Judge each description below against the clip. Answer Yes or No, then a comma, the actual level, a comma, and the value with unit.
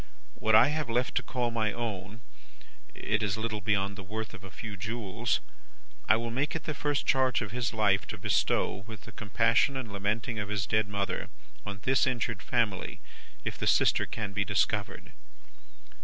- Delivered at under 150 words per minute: No, average, 185 wpm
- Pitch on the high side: No, low, 110 Hz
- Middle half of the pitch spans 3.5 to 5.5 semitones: No, average, 2.8 semitones